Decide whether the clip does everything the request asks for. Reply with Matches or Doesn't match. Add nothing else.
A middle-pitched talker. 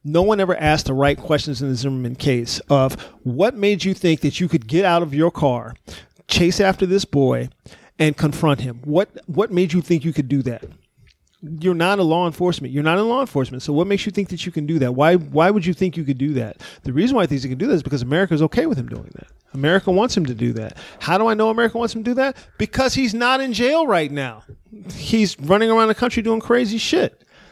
Matches